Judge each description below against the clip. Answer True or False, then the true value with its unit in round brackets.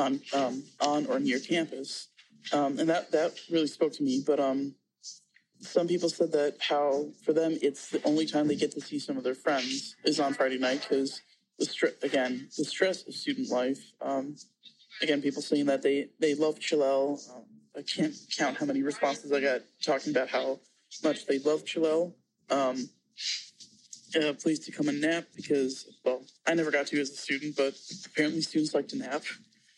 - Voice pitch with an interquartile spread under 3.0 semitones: True (2.5 semitones)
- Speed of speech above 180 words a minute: True (195 wpm)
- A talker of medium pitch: True (145 Hz)